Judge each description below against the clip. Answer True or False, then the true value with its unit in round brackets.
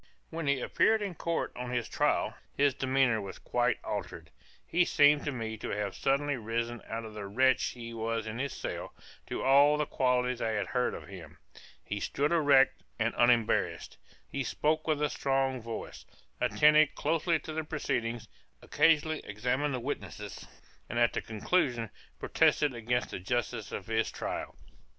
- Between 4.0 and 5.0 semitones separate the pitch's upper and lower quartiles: True (4.3 semitones)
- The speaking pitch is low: True (125 Hz)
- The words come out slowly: False (170 wpm)